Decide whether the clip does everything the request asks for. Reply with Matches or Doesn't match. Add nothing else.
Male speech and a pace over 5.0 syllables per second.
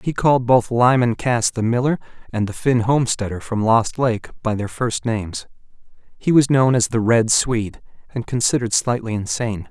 Matches